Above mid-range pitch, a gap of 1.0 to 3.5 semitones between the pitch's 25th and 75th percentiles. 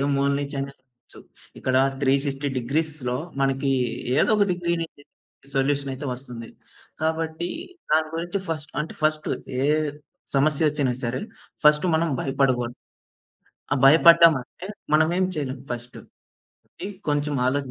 No: medium, 145 Hz; average, 3.0 semitones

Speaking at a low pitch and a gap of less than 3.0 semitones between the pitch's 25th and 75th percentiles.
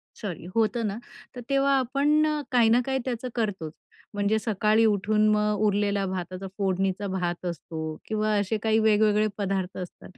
No: high, 210 Hz; narrow, 2.6 semitones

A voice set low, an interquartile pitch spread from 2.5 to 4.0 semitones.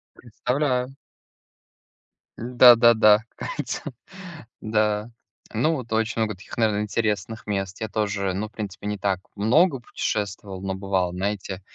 Yes: low, 105 Hz; average, 2.8 semitones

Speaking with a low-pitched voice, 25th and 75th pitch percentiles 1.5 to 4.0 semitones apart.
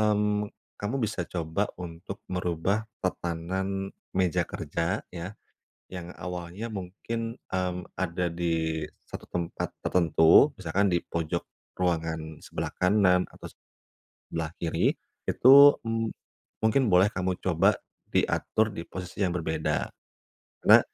Yes: very low, 90 Hz; average, 3.2 semitones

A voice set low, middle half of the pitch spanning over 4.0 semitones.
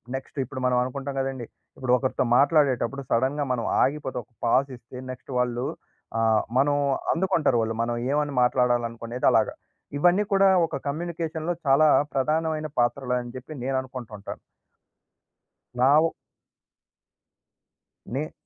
No: low, 130 Hz; average, 3.5 semitones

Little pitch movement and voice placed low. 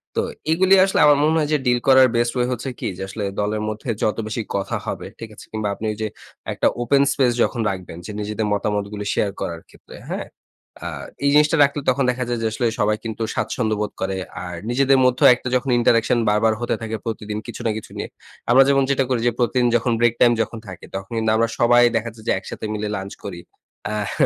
No: average, 3.1 semitones; low, 115 Hz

